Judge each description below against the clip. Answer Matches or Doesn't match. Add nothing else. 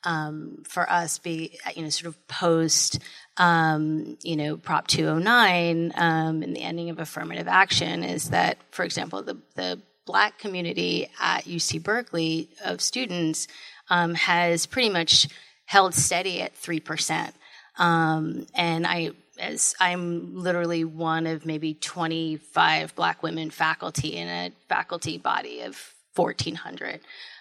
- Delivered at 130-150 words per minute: Matches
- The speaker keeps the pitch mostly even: Matches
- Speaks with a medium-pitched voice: Matches